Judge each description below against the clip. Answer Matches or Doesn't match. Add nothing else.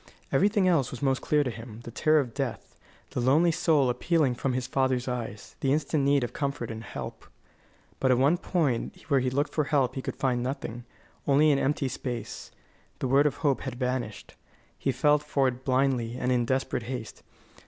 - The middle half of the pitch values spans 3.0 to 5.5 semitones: Doesn't match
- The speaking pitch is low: Matches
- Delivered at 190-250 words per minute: Matches